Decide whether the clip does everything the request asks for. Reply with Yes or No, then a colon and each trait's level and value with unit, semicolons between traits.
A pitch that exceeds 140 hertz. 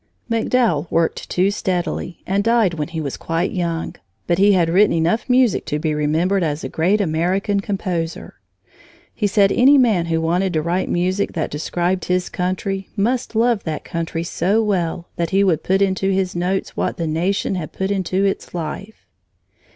Yes: medium, 185 Hz